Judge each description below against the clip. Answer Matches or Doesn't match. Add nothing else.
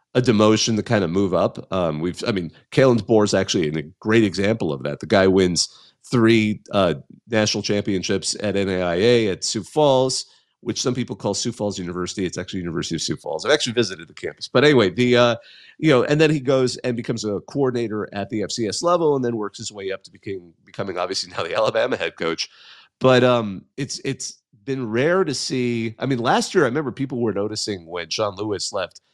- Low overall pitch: Matches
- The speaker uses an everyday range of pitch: Matches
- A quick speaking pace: Matches